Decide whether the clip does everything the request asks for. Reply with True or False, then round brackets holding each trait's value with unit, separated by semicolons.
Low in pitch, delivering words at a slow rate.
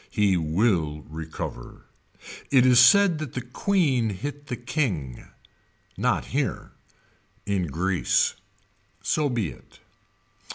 True (115 Hz; 110 wpm)